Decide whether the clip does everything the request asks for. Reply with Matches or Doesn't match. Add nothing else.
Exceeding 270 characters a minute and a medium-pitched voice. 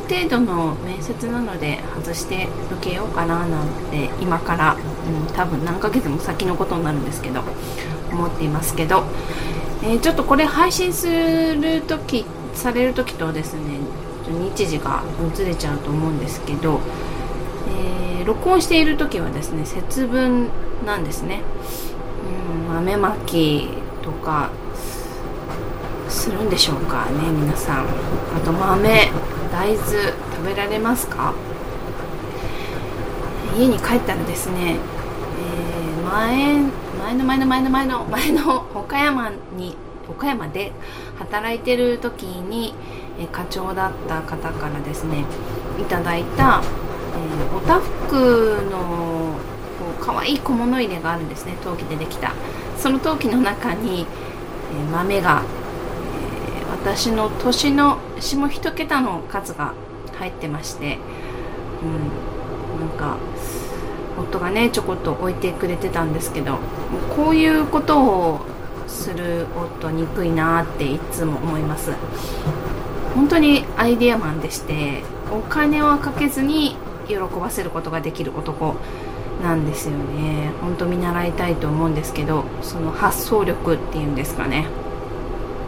Doesn't match